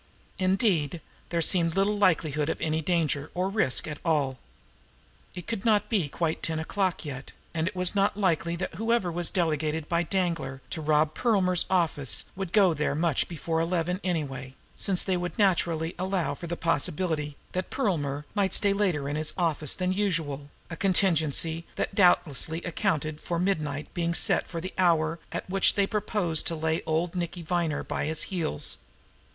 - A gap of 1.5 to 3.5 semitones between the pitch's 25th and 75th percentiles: Yes, average, 3.2 semitones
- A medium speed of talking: Yes, average, 175 wpm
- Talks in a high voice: No, medium, 170 Hz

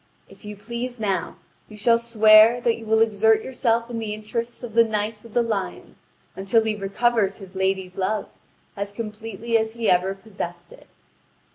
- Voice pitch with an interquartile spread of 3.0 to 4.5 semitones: No, narrow, 2.5 semitones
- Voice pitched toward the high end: Yes, high, 220 Hz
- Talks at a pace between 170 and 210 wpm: Yes, average, 175 wpm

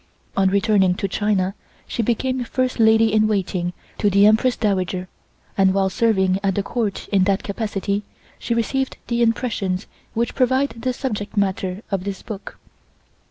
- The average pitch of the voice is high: Yes, high, 205 Hz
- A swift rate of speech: No, average, 160 wpm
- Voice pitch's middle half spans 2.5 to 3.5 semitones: Yes, average, 3.2 semitones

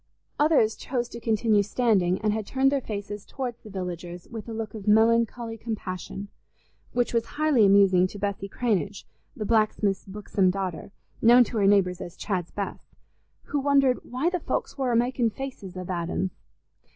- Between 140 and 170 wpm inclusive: Yes, average, 165 wpm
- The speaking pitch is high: Yes, high, 215 Hz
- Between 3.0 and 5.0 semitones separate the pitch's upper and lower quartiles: Yes, average, 3.7 semitones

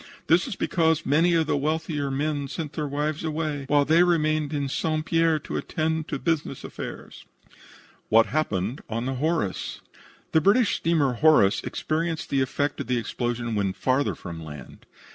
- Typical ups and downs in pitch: Yes, average, 3.4 semitones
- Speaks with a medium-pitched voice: Yes, medium, 150 Hz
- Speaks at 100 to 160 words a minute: No, average, 170 wpm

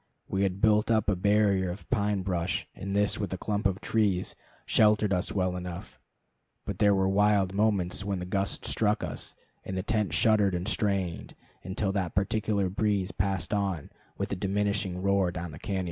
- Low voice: Yes, low, 100 Hz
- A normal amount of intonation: No, narrow, 2.0 semitones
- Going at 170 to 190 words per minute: Yes, average, 185 wpm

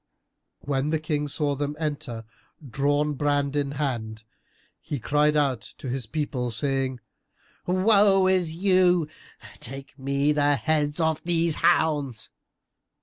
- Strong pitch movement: No, average, 2.7 semitones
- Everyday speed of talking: No, slow, 125 wpm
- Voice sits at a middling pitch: Yes, medium, 145 Hz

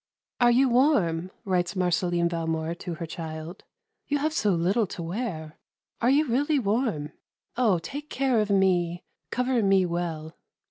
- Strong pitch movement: Yes, wide, 6.4 semitones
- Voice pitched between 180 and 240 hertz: Yes, medium, 185 Hz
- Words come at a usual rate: Yes, average, 150 wpm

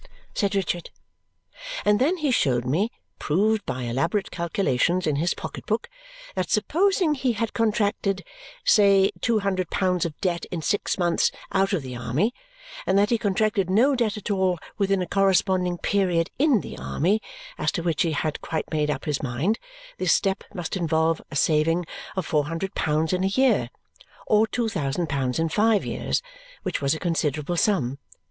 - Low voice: No, medium, 185 Hz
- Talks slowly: No, average, 175 wpm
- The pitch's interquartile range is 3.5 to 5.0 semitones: Yes, average, 4.6 semitones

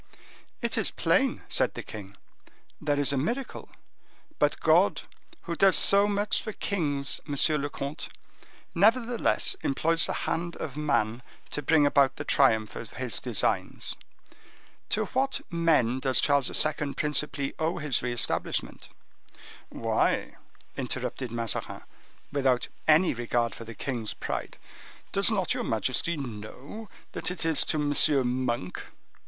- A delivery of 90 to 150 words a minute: Yes, slow, 135 wpm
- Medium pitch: Yes, medium, 145 Hz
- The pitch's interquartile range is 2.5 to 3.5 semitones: No, average, 4.9 semitones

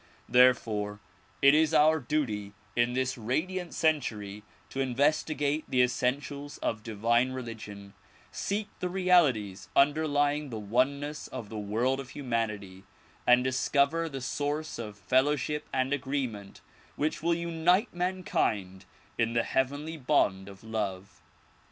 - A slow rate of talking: Yes, slow, 130 wpm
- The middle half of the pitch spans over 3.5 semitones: Yes, average, 5.3 semitones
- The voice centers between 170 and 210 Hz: No, low, 130 Hz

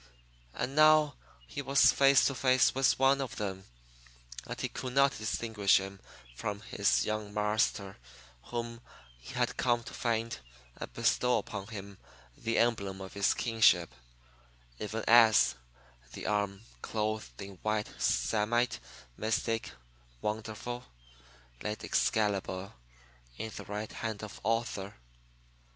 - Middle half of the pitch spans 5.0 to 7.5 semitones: No, average, 2.7 semitones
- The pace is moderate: No, slow, 125 wpm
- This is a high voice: No, low, 110 Hz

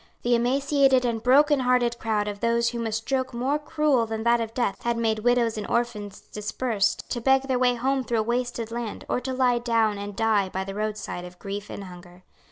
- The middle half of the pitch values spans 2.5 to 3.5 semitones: Yes, average, 2.9 semitones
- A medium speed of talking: No, fast, 210 wpm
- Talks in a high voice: Yes, high, 235 Hz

